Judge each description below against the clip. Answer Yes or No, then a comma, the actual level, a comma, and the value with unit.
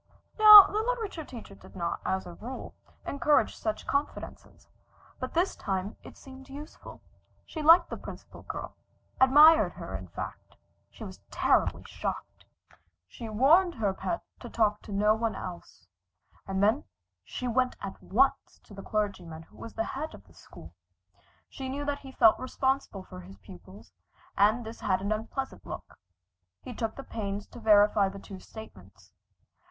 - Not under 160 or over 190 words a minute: Yes, average, 165 wpm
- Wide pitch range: Yes, wide, 5.9 semitones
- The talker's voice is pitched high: Yes, high, 220 Hz